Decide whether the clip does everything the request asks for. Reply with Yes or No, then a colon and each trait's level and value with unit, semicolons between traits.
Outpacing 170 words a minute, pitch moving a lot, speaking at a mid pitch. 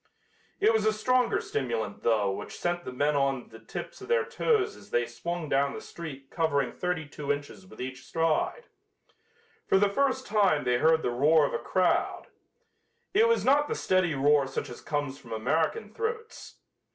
Yes: average, 190 wpm; wide, 7.8 semitones; medium, 160 Hz